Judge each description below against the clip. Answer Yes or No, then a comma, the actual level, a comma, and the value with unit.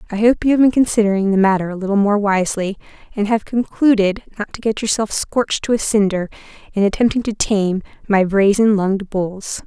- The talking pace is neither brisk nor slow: Yes, average, 190 wpm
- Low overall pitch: No, high, 205 Hz